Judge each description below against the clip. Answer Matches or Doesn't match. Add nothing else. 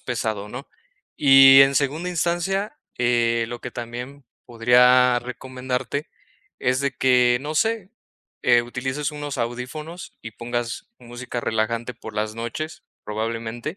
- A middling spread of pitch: Matches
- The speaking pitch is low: Matches